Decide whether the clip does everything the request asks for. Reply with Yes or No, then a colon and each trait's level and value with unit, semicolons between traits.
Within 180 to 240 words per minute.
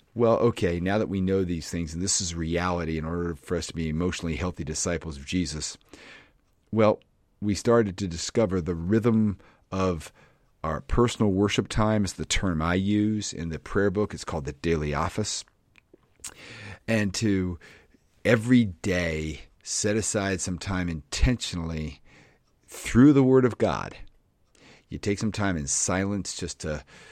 No: average, 155 wpm